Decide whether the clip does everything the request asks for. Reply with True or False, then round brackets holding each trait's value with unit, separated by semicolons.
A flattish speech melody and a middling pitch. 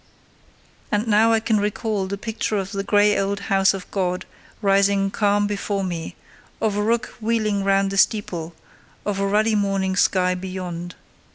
False (1.5 semitones; 200 Hz)